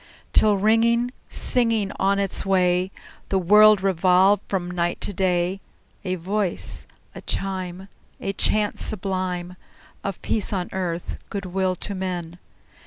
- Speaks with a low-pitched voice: No, high, 190 Hz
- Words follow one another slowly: Yes, slow, 130 wpm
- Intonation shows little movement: Yes, narrow, 2.0 semitones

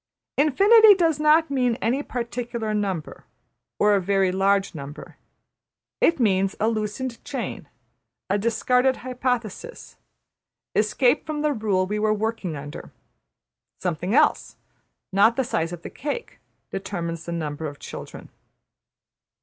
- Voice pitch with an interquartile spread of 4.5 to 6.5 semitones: Yes, wide, 5.5 semitones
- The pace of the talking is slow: Yes, slow, 130 wpm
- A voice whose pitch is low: No, high, 215 Hz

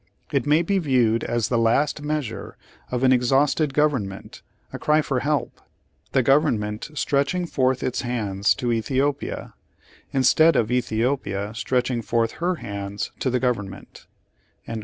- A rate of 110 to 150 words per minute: Yes, average, 140 wpm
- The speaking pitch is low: Yes, low, 125 Hz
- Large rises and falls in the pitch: No, average, 4.1 semitones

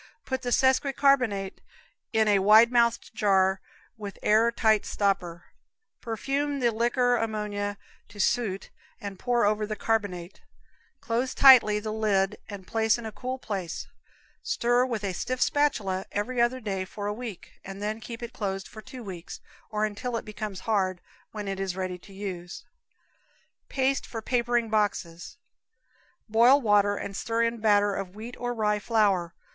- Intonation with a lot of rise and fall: No, average, 3.1 semitones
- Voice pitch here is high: Yes, high, 215 Hz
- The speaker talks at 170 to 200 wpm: No, average, 160 wpm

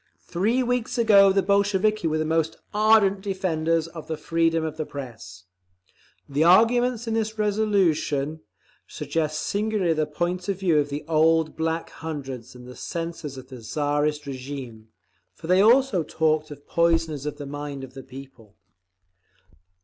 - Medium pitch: Yes, medium, 160 Hz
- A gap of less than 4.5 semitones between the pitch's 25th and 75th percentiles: No, average, 5.2 semitones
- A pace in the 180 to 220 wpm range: No, average, 150 wpm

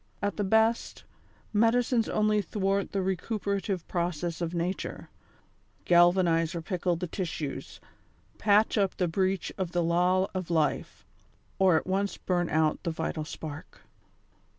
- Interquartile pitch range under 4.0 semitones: Yes, average, 2.9 semitones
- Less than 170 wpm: Yes, average, 140 wpm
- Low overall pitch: No, medium, 185 Hz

